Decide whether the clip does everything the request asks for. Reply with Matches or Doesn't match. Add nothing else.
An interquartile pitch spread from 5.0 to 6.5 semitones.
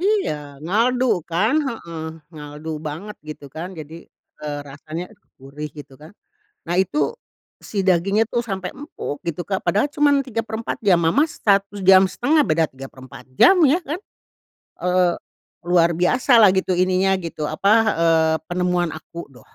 Matches